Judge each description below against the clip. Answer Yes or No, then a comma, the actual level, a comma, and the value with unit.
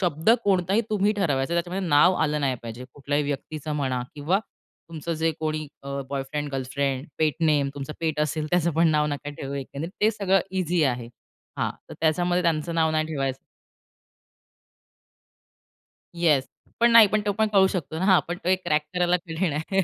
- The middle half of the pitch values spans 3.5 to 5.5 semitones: Yes, average, 3.9 semitones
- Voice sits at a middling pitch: Yes, medium, 160 Hz